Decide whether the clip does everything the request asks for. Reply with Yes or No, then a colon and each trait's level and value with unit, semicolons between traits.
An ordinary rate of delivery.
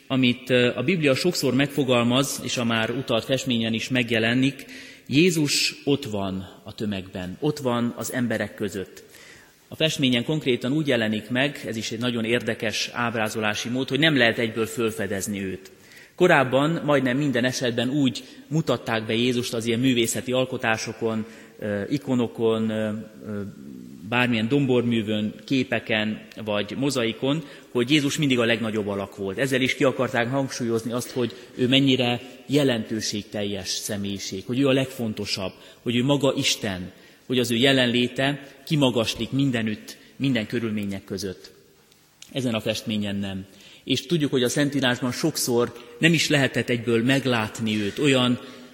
Yes: average, 135 wpm